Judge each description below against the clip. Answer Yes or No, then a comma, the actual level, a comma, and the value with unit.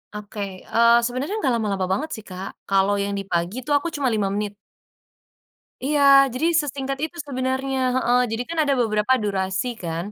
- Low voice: No, high, 230 Hz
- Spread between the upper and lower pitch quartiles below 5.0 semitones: No, average, 5.3 semitones